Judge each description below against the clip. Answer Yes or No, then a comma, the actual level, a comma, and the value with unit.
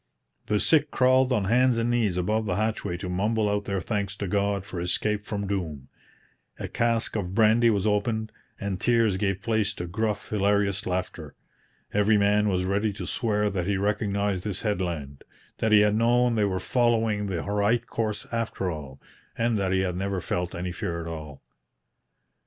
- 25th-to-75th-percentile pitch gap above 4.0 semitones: No, average, 2.8 semitones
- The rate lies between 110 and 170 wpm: No, average, 180 wpm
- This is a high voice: No, low, 105 Hz